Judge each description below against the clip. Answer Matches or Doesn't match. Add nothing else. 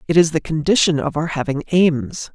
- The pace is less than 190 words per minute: Doesn't match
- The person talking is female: Doesn't match